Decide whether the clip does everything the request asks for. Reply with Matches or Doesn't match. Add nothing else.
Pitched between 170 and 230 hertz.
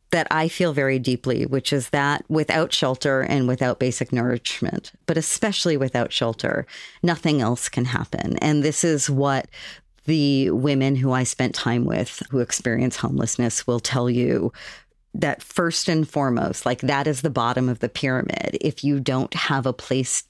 Doesn't match